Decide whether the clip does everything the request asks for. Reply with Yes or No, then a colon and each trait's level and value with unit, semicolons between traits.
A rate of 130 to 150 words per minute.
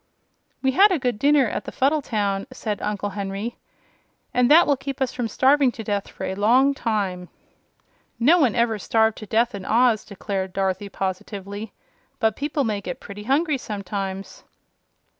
No: average, 170 wpm